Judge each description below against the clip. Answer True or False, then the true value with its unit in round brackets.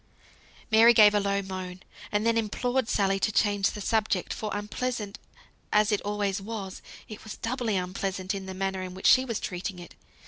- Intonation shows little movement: True (2.3 semitones)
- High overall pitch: True (205 Hz)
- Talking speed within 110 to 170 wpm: False (185 wpm)